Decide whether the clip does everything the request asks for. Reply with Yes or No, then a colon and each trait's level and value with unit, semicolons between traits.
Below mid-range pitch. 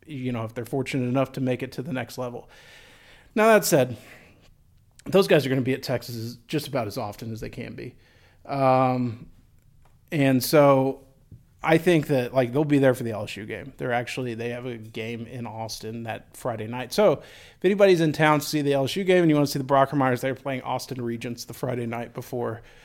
Yes: low, 130 Hz